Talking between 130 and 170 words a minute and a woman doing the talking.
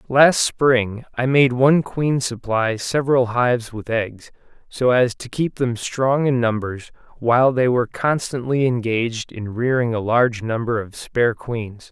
No: average, 160 wpm; male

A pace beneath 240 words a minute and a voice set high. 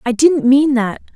Yes: fast, 205 wpm; very high, 265 Hz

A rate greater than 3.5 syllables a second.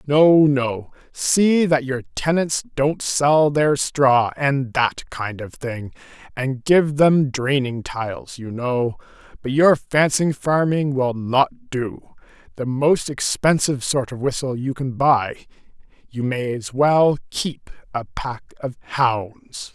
No: 3.4 syllables/s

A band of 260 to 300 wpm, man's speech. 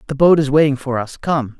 Yes: fast, 265 wpm; male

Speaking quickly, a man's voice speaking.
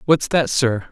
No: average, 195 wpm; male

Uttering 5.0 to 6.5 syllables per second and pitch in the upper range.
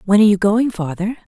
Yes: 6.0 syllables/s; high, 205 Hz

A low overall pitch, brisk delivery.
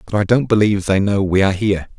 Yes: low, 100 Hz; fast, 270 wpm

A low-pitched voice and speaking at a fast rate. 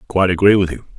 Yes: very low, 95 Hz; fast, 305 wpm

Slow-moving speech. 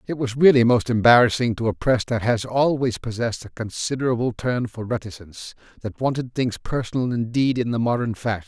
No: average, 185 wpm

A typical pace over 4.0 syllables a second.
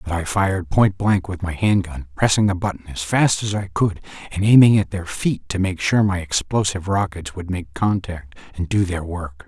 Yes: 5.1 syllables/s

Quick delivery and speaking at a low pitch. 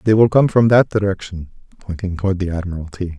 No: average, 190 wpm; very low, 95 Hz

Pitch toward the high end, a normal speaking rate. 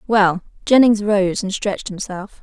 Yes: high, 200 Hz; average, 150 wpm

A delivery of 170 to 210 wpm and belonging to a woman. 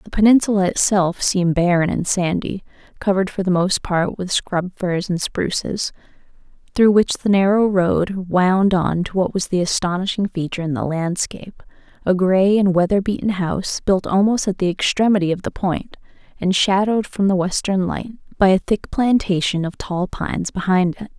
Yes: average, 175 wpm; female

